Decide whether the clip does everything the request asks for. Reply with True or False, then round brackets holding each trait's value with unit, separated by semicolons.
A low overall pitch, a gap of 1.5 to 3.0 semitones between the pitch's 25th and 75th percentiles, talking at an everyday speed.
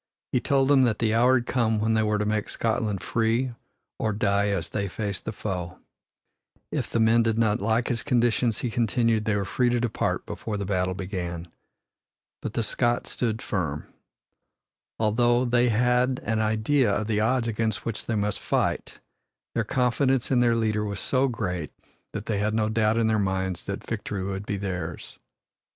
True (110 Hz; 2.7 semitones; 185 wpm)